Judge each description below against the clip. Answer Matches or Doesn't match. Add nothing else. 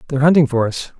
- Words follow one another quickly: Matches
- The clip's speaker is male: Matches